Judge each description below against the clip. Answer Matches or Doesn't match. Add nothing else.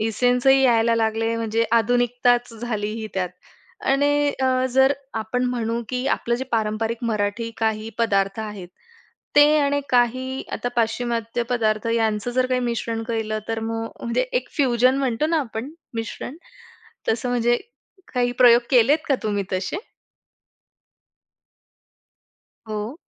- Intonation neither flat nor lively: Doesn't match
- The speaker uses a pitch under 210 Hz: Doesn't match